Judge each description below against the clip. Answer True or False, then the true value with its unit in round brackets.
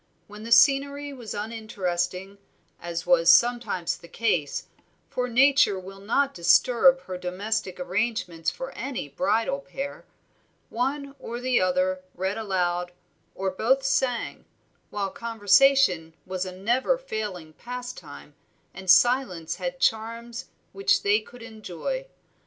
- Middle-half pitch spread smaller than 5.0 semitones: False (5.5 semitones)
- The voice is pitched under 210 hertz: False (215 Hz)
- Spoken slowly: True (125 wpm)